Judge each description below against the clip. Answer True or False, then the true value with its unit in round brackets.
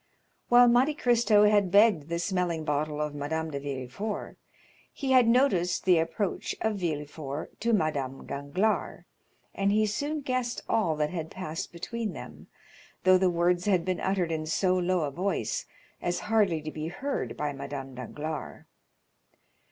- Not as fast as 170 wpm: True (155 wpm)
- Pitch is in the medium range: True (175 Hz)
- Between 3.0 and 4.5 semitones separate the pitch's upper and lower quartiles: False (5.4 semitones)